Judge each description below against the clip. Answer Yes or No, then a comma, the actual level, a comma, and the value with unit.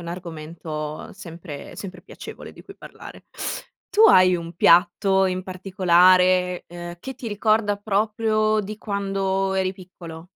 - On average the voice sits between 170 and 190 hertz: Yes, medium, 185 Hz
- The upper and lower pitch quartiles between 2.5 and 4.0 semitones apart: Yes, average, 2.8 semitones